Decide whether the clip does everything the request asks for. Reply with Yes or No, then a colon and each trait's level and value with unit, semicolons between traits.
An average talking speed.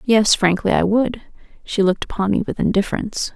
Yes: average, 180 wpm